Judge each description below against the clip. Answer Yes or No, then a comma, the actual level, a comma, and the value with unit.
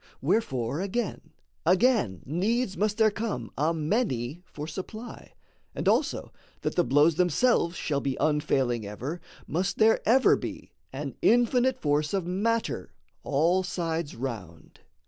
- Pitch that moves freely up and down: Yes, wide, 7.0 semitones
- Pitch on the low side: No, medium, 170 Hz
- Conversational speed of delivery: No, slow, 130 wpm